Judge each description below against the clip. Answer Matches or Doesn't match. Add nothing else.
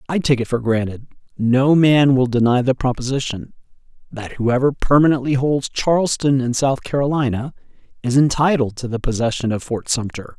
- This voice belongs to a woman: Doesn't match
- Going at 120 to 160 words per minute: Matches